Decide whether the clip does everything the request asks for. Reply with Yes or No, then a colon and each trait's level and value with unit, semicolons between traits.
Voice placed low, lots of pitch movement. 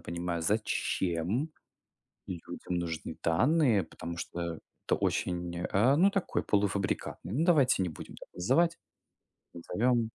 Yes: very low, 95 Hz; wide, 6.7 semitones